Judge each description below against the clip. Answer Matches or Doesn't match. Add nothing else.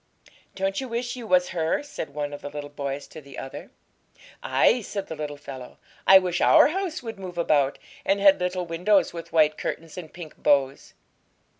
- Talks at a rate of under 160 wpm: Doesn't match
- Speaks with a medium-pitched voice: Matches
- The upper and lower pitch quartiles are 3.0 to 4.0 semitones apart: Doesn't match